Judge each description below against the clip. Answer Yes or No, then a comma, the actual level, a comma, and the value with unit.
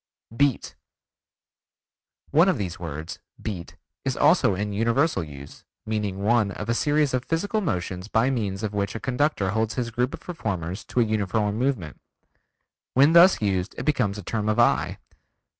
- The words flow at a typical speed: Yes, average, 165 wpm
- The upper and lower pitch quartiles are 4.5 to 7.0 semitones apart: Yes, average, 5.3 semitones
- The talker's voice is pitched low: Yes, low, 110 Hz